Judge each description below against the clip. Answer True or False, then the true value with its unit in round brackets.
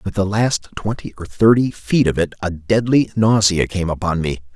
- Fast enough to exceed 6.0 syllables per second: False (4.9 syllables/s)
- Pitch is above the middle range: False (100 Hz)